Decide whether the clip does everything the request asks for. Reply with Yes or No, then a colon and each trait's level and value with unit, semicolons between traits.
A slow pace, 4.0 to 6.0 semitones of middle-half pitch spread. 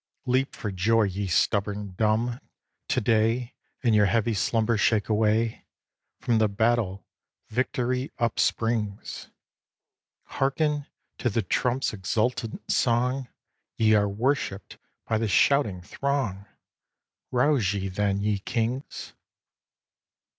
No: slow, 110 wpm; average, 3.3 semitones